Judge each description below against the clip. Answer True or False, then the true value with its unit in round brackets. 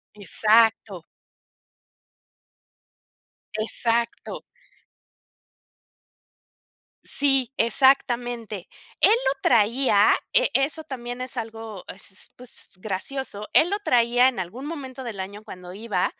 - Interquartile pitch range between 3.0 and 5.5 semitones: True (4.0 semitones)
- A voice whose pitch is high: True (235 Hz)